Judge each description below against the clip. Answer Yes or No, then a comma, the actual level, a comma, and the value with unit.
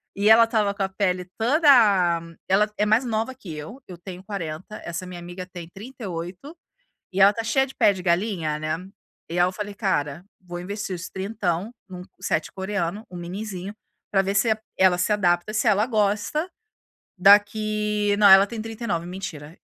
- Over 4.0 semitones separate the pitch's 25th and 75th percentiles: No, average, 3.2 semitones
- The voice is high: Yes, high, 195 Hz